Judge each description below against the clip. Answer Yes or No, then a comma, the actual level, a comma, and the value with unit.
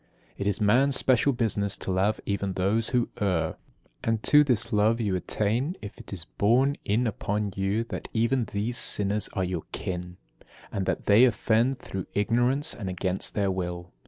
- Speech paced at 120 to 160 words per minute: No, average, 180 wpm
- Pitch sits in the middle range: No, low, 105 Hz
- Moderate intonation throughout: Yes, average, 3.6 semitones